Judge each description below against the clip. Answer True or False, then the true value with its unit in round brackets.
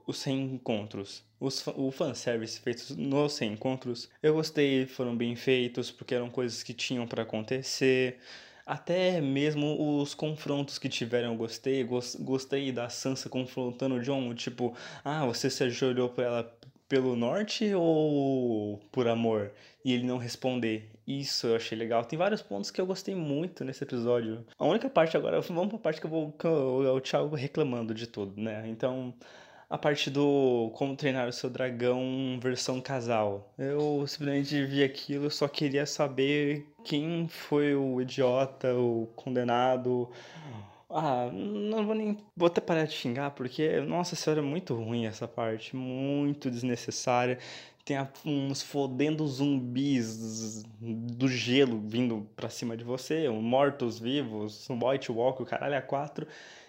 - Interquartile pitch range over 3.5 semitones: False (3.2 semitones)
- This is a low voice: True (130 Hz)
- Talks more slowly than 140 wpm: False (155 wpm)